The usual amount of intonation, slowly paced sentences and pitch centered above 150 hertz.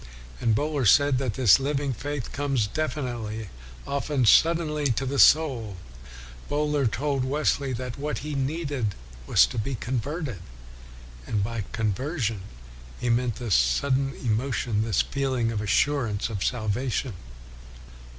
No: average, 4.3 semitones; slow, 130 wpm; low, 130 Hz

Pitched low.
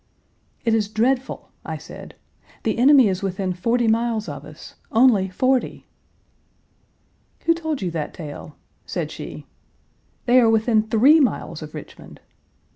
No: high, 220 Hz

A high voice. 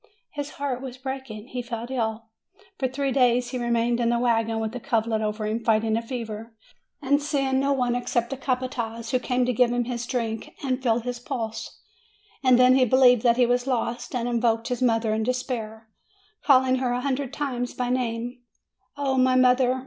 Yes: high, 245 Hz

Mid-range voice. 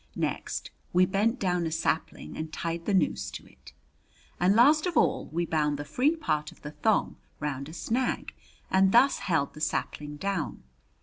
Yes: medium, 175 Hz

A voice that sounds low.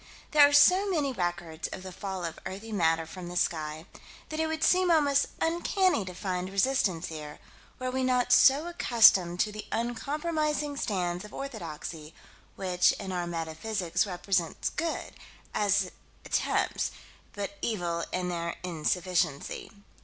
No: high, 190 Hz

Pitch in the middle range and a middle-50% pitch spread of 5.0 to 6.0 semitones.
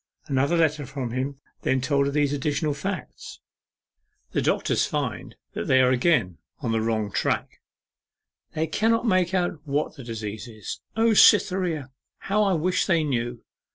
Yes: medium, 145 Hz; wide, 5.6 semitones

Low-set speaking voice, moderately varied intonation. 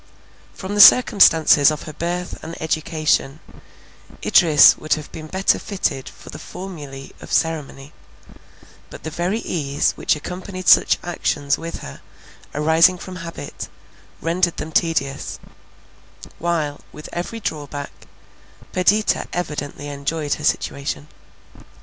No: medium, 160 Hz; average, 3.4 semitones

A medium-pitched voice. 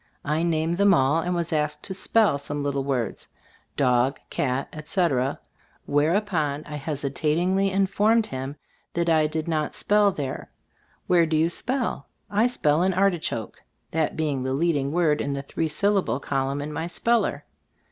Yes: medium, 155 Hz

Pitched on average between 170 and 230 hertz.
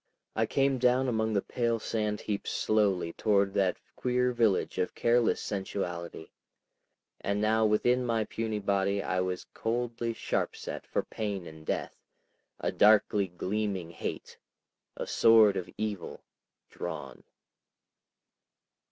No: low, 105 Hz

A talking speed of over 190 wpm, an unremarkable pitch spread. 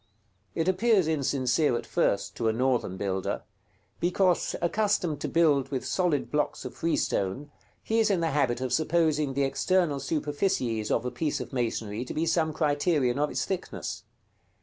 No: average, 165 wpm; average, 5.0 semitones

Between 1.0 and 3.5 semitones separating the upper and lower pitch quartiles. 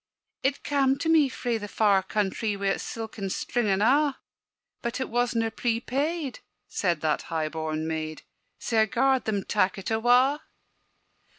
No: average, 5.1 semitones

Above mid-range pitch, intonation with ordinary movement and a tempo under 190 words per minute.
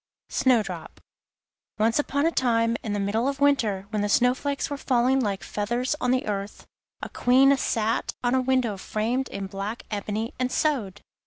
Yes: high, 235 Hz; average, 4.0 semitones; average, 175 wpm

